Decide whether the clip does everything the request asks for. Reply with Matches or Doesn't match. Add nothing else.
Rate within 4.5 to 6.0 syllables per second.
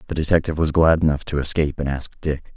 Doesn't match